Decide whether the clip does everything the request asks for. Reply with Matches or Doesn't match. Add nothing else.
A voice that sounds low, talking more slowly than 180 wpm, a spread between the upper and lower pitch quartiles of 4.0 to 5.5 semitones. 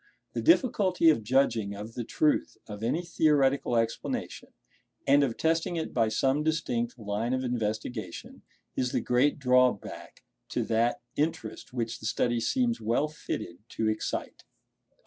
Matches